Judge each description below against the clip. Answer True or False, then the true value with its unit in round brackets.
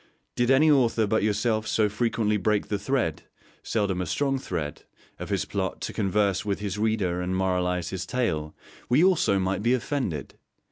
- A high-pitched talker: False (105 Hz)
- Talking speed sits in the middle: True (175 wpm)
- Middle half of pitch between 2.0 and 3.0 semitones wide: False (4.2 semitones)